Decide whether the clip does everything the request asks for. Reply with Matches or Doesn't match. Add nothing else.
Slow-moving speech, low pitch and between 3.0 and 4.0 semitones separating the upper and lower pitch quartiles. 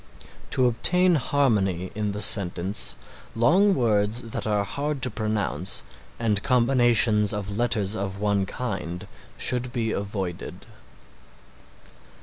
Matches